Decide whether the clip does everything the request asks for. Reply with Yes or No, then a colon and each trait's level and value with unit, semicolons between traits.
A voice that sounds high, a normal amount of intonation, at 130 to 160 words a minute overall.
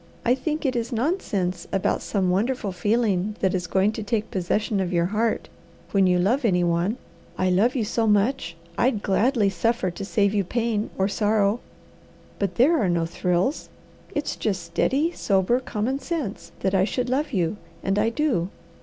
No: high, 210 Hz; average, 4.5 semitones; average, 180 wpm